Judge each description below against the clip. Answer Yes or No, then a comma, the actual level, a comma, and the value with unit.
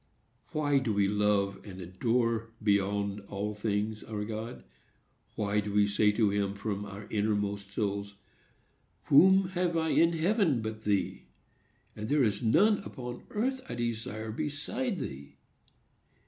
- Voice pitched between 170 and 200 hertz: No, low, 110 Hz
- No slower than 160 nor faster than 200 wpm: No, average, 140 wpm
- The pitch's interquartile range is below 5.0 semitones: No, wide, 5.4 semitones